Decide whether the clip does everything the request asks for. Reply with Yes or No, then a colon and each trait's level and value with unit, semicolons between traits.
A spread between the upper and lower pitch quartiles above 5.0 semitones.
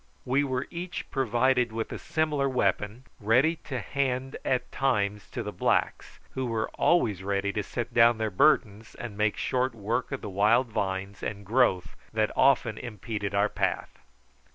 No: average, 4.1 semitones